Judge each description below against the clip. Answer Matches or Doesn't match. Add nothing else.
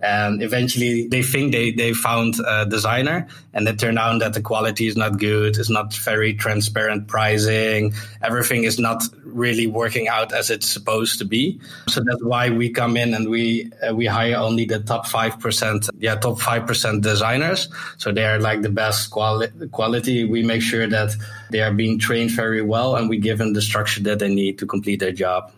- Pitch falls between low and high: Doesn't match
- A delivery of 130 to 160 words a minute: Doesn't match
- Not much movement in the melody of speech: Matches